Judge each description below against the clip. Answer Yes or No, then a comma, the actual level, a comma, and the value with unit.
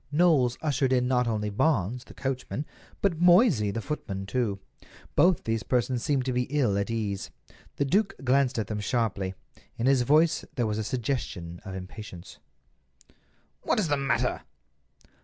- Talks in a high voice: No, low, 125 Hz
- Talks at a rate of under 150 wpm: No, average, 160 wpm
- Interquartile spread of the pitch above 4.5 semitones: Yes, average, 5.0 semitones